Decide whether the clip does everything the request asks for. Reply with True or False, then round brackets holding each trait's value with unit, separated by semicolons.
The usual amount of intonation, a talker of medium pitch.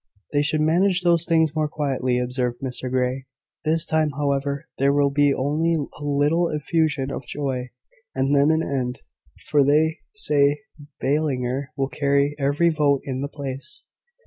False (2.3 semitones; 145 Hz)